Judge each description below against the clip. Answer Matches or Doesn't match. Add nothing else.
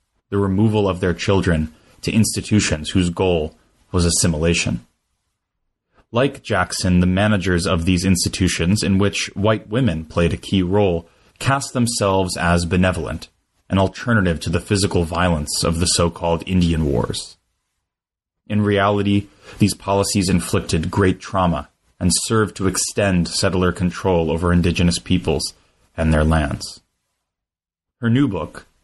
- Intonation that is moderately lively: Matches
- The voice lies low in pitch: Matches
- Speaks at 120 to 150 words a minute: Matches